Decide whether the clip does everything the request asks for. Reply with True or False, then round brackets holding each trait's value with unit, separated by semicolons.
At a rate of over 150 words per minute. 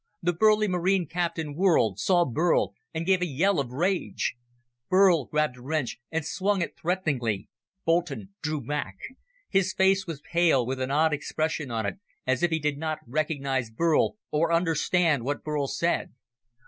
True (165 wpm)